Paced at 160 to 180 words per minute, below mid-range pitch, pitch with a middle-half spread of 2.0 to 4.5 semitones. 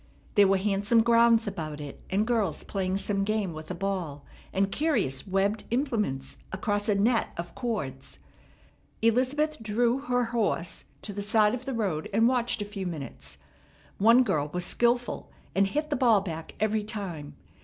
No: average, 165 wpm; high, 205 Hz; average, 4.2 semitones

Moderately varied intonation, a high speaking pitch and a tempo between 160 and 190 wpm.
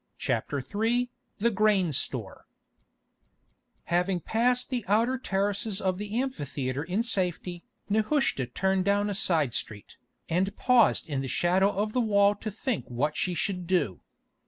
No: average, 3.9 semitones; high, 195 Hz; average, 145 wpm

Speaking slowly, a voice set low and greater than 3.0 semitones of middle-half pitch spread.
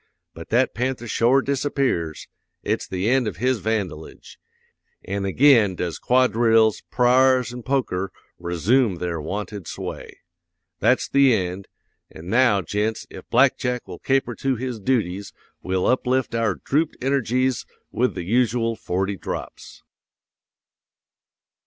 Yes: slow, 125 wpm; low, 115 Hz; average, 4.9 semitones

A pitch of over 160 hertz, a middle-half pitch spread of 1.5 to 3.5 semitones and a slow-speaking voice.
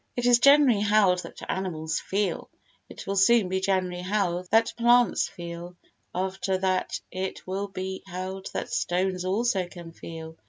No: high, 190 Hz; narrow, 2.4 semitones; average, 155 wpm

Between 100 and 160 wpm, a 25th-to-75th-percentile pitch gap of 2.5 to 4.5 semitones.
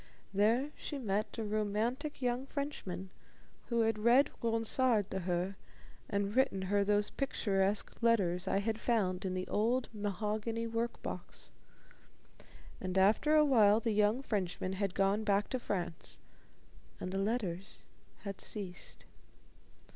Yes: slow, 135 wpm; average, 3.2 semitones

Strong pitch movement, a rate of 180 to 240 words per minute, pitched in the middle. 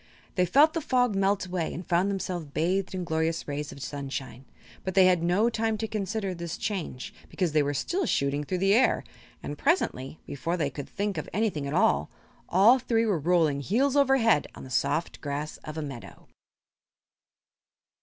Yes: wide, 6.1 semitones; average, 185 wpm; medium, 180 Hz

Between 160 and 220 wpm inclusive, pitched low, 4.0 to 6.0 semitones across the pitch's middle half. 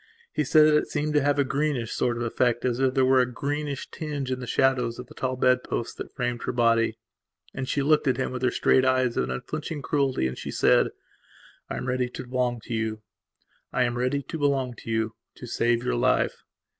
No: average, 200 wpm; low, 130 Hz; narrow, 2.6 semitones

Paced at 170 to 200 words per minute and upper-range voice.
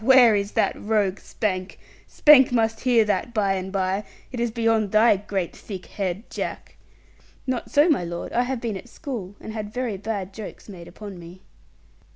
Yes: average, 185 wpm; high, 215 Hz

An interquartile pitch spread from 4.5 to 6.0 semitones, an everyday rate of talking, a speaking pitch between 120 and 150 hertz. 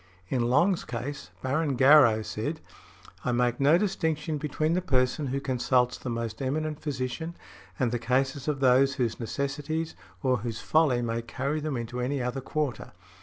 No: average, 3.6 semitones; average, 165 wpm; low, 135 Hz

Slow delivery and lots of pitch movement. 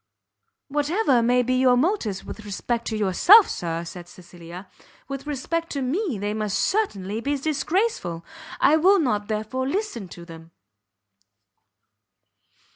Yes: slow, 130 wpm; wide, 7.4 semitones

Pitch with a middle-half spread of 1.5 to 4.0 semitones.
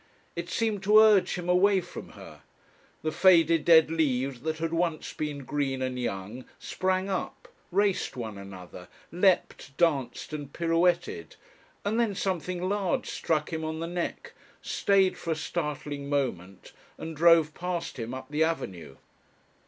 No: average, 4.7 semitones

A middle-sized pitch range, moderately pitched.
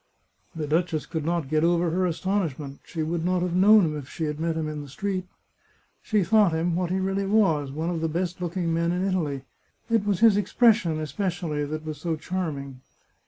Yes: average, 3.2 semitones; medium, 170 Hz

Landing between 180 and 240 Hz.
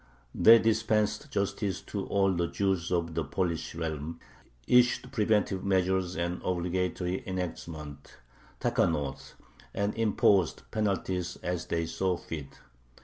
No: very low, 90 Hz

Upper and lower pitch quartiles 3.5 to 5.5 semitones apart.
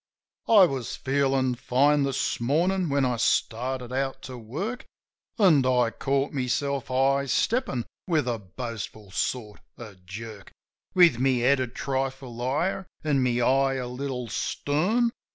No: average, 2.7 semitones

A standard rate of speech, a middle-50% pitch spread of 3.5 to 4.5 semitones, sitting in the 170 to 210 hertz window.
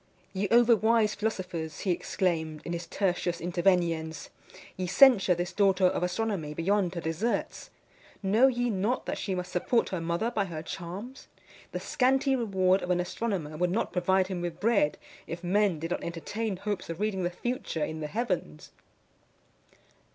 Yes: average, 165 wpm; average, 3.8 semitones; medium, 185 Hz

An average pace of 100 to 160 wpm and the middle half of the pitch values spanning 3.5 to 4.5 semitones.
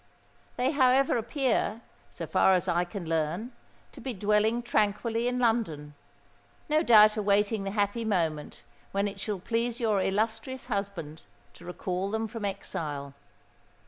Yes: average, 140 wpm; average, 3.9 semitones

